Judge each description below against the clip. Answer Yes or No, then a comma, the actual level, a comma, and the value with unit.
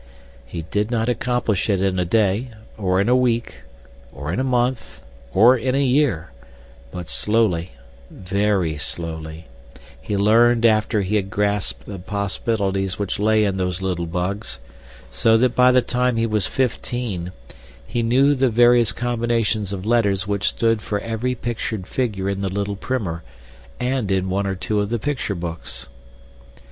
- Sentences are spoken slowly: No, average, 160 wpm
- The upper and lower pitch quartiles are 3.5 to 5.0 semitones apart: Yes, average, 3.9 semitones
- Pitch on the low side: Yes, low, 105 Hz